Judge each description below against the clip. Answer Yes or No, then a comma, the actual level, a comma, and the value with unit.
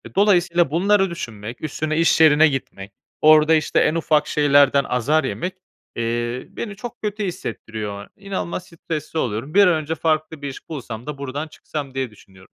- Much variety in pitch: No, average, 4.5 semitones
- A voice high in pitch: No, medium, 155 Hz